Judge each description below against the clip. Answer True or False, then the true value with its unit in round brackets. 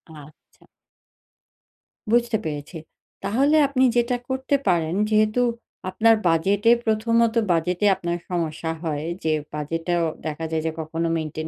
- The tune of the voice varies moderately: False (6.0 semitones)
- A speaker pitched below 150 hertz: False (175 Hz)